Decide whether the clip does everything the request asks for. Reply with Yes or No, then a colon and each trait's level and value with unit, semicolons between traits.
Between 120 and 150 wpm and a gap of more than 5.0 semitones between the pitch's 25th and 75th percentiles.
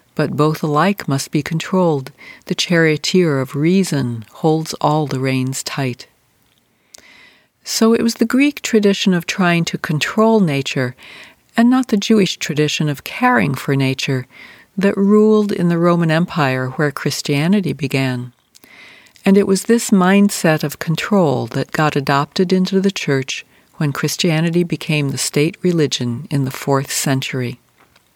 Yes: average, 145 wpm; wide, 5.6 semitones